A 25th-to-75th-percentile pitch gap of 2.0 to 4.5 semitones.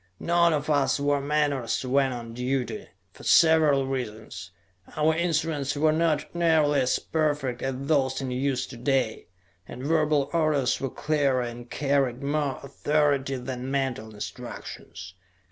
Yes: average, 2.8 semitones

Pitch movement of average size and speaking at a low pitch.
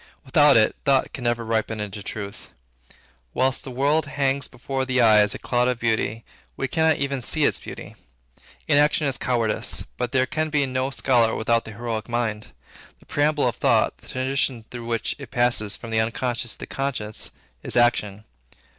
Yes: average, 3.3 semitones; low, 125 Hz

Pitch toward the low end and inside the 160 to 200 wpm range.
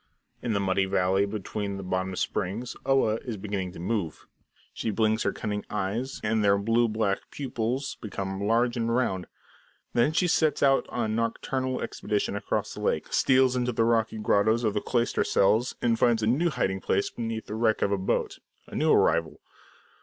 Yes: low, 110 Hz; average, 185 wpm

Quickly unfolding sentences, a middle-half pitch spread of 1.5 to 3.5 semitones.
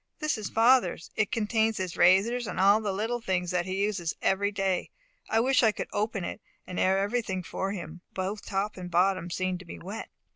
Yes: fast, 210 wpm; average, 3.0 semitones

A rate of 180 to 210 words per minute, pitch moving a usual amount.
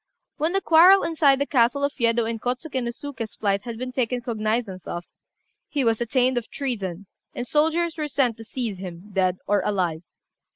Yes: average, 190 wpm; average, 5.0 semitones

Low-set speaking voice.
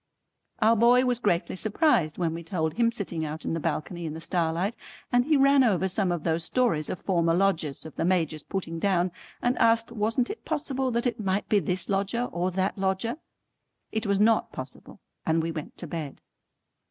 No: high, 190 Hz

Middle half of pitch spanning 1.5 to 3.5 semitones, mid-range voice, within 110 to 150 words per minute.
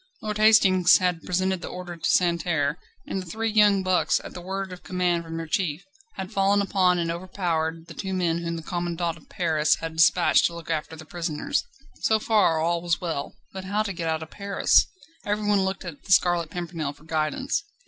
No: average, 2.7 semitones; medium, 175 Hz; fast, 205 wpm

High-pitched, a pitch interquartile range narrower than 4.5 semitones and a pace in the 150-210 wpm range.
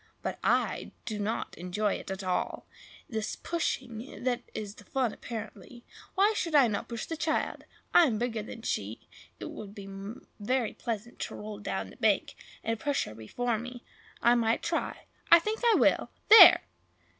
Yes: high, 230 Hz; average, 3.5 semitones; average, 180 wpm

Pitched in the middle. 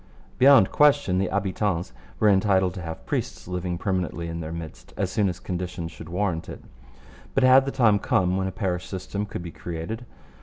No: very low, 95 Hz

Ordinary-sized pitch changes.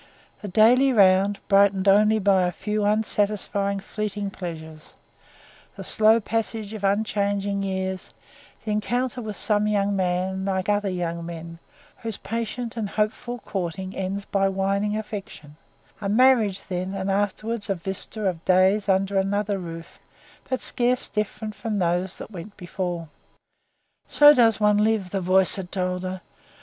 No: narrow, 2.2 semitones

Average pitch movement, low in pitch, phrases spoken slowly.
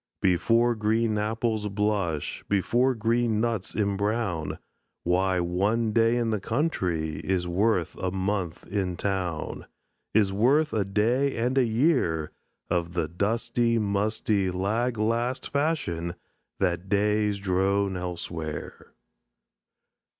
Yes: average, 4.1 semitones; low, 105 Hz; slow, 115 wpm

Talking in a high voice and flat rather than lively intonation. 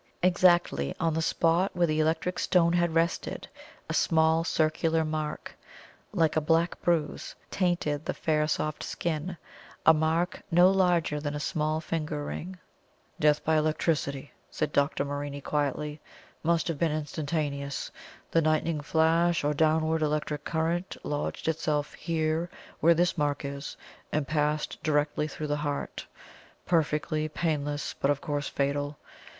No: medium, 155 Hz; narrow, 2.0 semitones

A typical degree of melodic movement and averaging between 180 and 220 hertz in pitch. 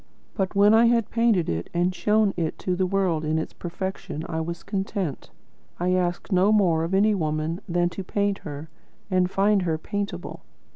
Yes: average, 3.4 semitones; medium, 185 Hz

